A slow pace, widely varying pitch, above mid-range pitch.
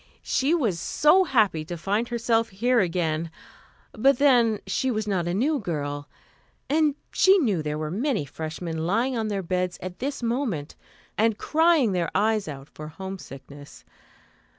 No: average, 155 wpm; wide, 7.0 semitones; high, 205 Hz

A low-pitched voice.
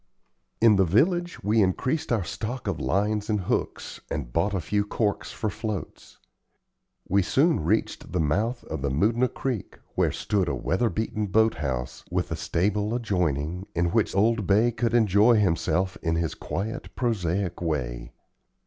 Yes: low, 100 Hz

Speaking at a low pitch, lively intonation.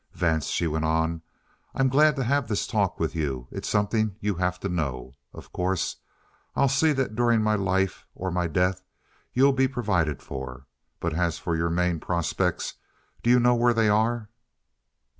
Yes: very low, 95 Hz; wide, 6.2 semitones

